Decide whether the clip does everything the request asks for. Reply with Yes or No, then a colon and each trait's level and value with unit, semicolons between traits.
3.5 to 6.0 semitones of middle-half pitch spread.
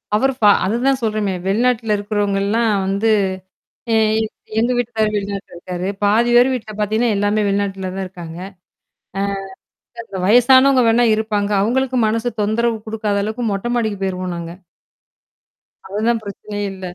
No: average, 2.8 semitones